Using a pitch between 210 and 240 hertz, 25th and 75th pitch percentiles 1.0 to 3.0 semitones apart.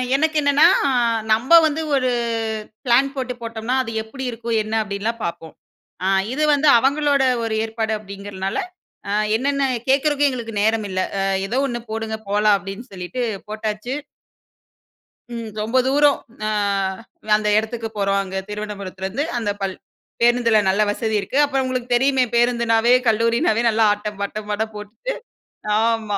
No: high, 225 Hz; average, 3.5 semitones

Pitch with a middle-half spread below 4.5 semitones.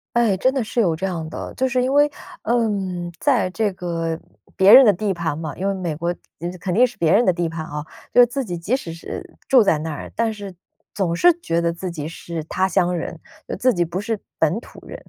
No: average, 5.1 semitones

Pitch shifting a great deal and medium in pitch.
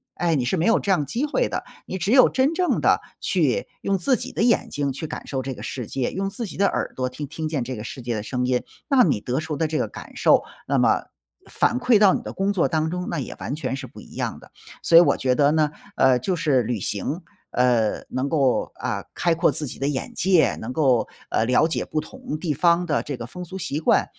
Yes: wide, 6.4 semitones; medium, 155 Hz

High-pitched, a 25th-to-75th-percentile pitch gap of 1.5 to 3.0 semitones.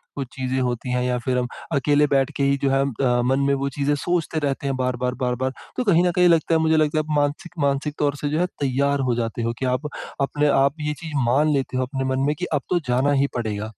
No: medium, 140 Hz; average, 2.7 semitones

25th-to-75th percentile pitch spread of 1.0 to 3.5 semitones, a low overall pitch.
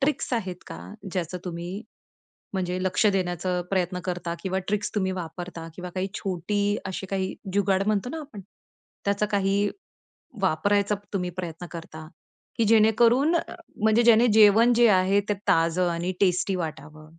No: average, 2.8 semitones; high, 190 Hz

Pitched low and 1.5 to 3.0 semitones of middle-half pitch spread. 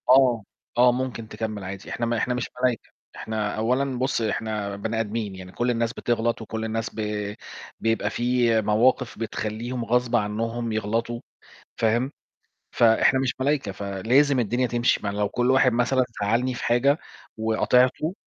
Yes: low, 115 Hz; narrow, 2.5 semitones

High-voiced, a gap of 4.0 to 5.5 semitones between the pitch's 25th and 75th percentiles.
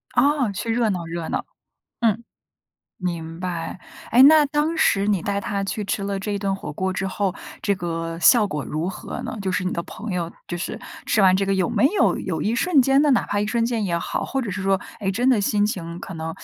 Yes: high, 195 Hz; average, 4.3 semitones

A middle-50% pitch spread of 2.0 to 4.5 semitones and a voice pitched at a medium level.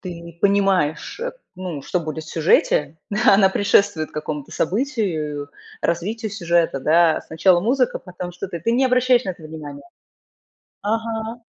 No: wide, 5.6 semitones; medium, 180 Hz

